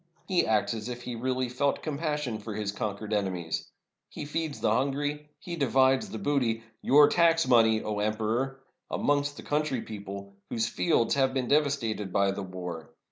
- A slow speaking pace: No, average, 180 wpm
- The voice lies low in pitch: Yes, low, 125 Hz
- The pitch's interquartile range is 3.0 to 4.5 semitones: No, average, 5.1 semitones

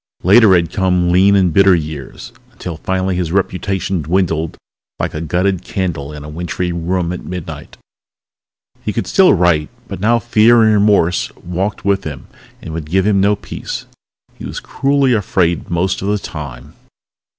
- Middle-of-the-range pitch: No, very low, 90 Hz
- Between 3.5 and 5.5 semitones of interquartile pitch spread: No, average, 3.0 semitones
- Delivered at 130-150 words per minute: No, average, 165 wpm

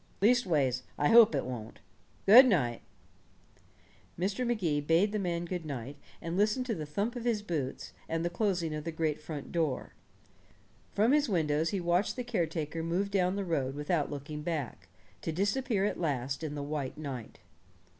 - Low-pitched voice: No, medium, 165 Hz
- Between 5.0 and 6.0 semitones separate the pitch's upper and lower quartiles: Yes, wide, 5.4 semitones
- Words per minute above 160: Yes, average, 175 wpm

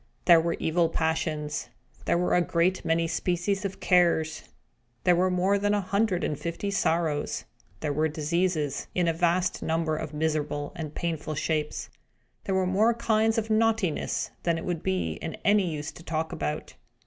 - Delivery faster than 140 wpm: Yes, average, 170 wpm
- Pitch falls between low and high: Yes, medium, 170 Hz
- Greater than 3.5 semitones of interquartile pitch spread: No, average, 3.0 semitones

